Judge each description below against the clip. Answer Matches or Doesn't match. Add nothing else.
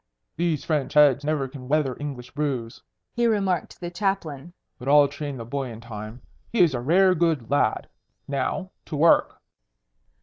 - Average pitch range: Matches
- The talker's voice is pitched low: Doesn't match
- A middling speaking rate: Matches